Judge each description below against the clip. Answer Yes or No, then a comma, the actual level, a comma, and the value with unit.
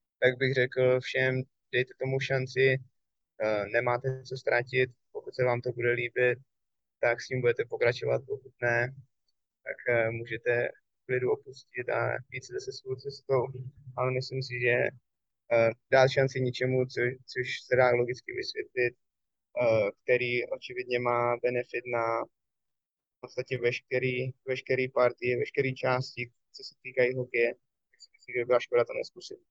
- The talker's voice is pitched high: No, low, 130 Hz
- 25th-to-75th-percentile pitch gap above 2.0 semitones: No, narrow, 1.5 semitones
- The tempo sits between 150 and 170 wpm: No, average, 135 wpm